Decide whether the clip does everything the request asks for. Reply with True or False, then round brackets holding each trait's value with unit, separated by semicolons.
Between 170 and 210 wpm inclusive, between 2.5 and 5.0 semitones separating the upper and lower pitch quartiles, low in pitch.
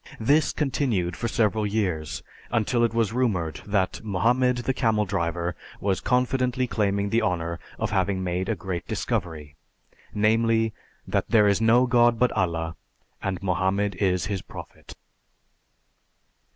False (140 wpm; 4.2 semitones; 105 Hz)